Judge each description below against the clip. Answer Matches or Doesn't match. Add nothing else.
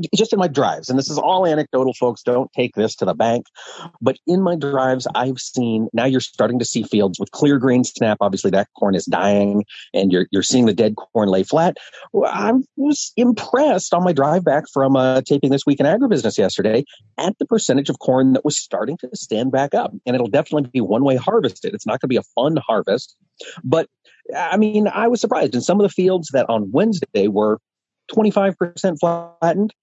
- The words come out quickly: Matches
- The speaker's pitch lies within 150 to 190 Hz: Doesn't match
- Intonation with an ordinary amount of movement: Doesn't match